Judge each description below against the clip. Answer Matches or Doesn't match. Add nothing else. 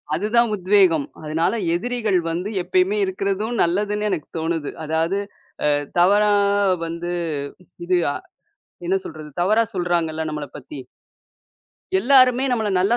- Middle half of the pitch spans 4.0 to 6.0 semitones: Matches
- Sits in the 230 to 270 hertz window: Doesn't match